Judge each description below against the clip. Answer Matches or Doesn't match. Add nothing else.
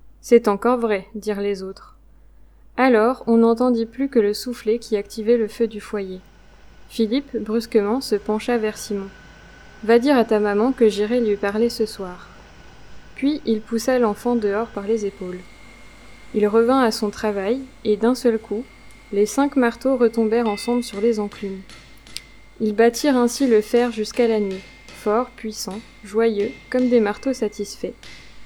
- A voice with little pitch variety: Matches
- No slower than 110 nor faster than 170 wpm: Matches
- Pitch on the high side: Matches